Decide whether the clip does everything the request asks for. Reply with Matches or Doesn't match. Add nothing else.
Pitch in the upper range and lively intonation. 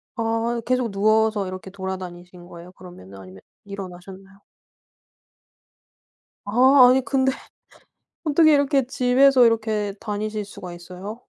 Doesn't match